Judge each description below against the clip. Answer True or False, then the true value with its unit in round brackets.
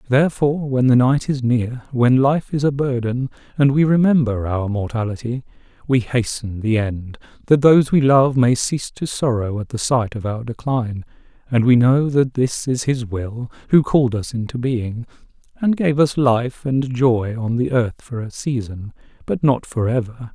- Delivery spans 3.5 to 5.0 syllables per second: True (4.7 syllables/s)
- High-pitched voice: False (125 Hz)